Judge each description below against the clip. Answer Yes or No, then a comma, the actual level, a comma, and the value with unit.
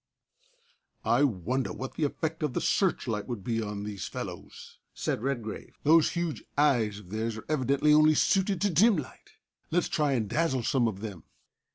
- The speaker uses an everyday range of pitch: No, wide, 6.0 semitones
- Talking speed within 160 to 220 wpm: Yes, average, 175 wpm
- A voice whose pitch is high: No, low, 135 Hz